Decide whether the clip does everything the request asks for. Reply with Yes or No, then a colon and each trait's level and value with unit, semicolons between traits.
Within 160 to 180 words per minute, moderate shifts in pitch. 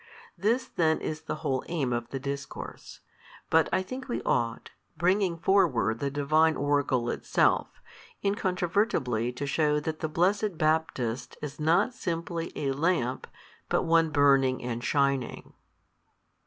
No: slow, 135 wpm; average, 4.2 semitones